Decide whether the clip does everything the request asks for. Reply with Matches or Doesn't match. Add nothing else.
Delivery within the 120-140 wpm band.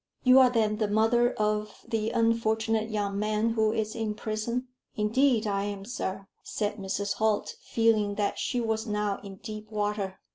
Doesn't match